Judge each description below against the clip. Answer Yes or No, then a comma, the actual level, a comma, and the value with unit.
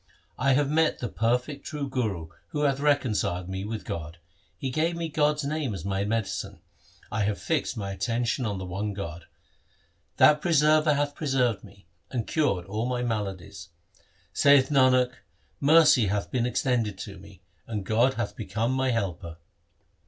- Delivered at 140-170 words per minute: Yes, average, 160 wpm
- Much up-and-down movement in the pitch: Yes, wide, 6.0 semitones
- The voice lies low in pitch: Yes, low, 120 Hz